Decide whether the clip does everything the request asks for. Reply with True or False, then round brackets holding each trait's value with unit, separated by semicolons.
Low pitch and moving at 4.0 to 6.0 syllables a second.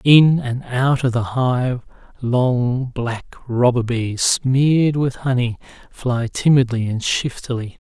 False (125 Hz; 3.5 syllables/s)